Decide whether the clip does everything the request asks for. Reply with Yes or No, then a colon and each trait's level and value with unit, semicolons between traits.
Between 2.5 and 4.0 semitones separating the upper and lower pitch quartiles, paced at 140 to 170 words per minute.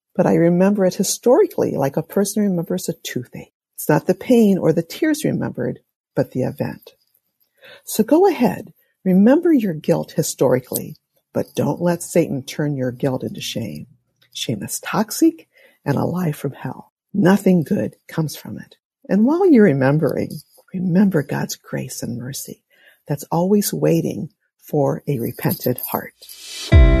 No: average, 5.2 semitones; average, 150 wpm